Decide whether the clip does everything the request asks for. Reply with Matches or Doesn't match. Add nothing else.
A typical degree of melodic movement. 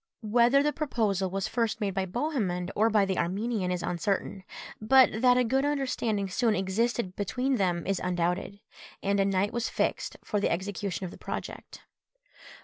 Matches